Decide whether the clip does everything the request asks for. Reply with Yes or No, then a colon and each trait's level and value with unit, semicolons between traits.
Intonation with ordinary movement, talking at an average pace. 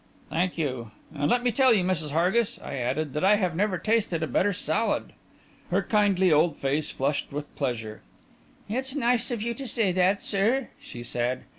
No: wide, 7.1 semitones; average, 185 wpm